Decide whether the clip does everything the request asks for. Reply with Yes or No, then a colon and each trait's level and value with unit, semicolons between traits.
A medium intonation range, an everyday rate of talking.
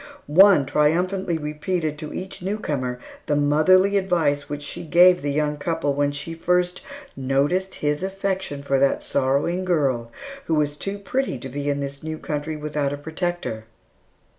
Yes: average, 3.8 semitones; average, 160 wpm